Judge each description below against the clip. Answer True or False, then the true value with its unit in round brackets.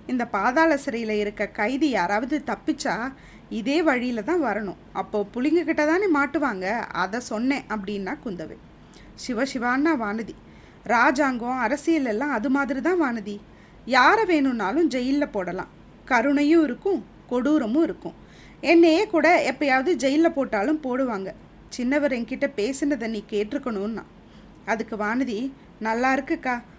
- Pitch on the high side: True (260 Hz)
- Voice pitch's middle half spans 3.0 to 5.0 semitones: False (5.4 semitones)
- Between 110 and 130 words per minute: True (115 wpm)